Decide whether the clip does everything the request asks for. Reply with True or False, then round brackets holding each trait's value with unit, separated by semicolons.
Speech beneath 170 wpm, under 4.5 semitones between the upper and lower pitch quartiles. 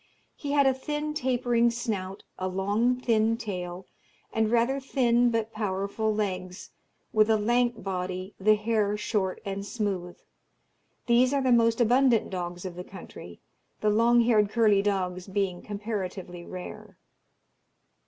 True (140 wpm; 3.9 semitones)